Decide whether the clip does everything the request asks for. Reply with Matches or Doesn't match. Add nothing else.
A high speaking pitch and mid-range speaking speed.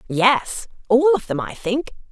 Matches